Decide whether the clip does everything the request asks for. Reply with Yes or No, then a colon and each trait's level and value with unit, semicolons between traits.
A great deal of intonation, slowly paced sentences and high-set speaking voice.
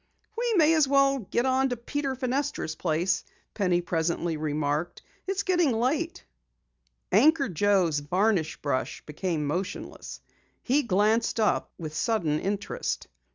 Yes: wide, 8.7 semitones; slow, 125 wpm; high, 205 Hz